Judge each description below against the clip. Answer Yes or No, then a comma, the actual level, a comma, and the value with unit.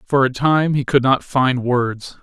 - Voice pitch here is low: Yes, low, 130 Hz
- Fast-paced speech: Yes, fast, 215 wpm